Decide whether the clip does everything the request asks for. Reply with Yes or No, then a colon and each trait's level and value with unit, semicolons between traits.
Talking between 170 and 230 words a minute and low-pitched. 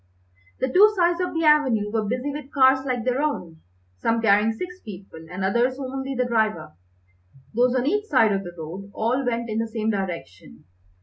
No: average, 190 wpm; high, 235 Hz